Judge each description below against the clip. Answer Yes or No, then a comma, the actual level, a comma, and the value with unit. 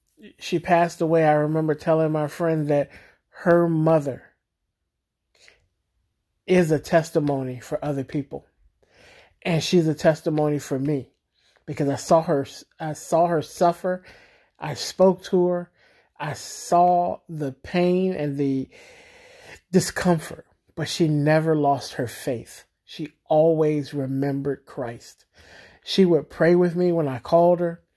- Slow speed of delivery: Yes, slow, 130 wpm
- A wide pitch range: No, average, 3.3 semitones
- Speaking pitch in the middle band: Yes, medium, 160 Hz